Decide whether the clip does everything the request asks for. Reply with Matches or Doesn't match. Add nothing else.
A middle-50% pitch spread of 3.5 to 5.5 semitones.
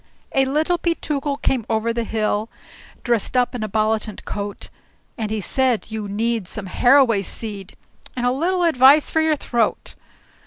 Matches